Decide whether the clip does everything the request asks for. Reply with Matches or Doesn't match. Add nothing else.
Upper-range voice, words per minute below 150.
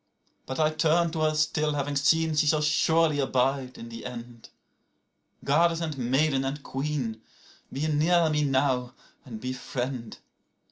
Doesn't match